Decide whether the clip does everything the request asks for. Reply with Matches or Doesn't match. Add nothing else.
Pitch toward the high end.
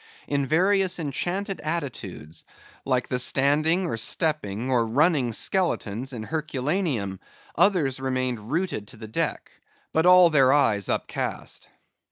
Doesn't match